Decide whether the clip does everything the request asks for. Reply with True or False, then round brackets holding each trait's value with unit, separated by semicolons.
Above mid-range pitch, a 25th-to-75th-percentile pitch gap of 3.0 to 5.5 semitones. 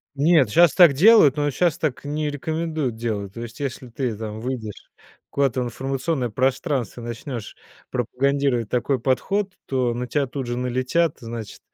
False (130 Hz; 3.5 semitones)